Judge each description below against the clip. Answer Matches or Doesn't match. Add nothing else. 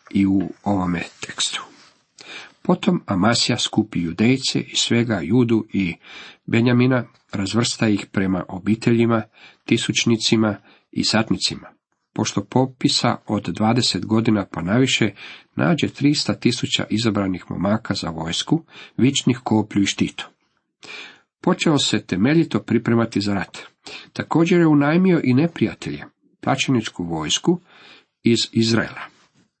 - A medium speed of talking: Doesn't match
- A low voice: Matches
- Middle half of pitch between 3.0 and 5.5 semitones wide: Matches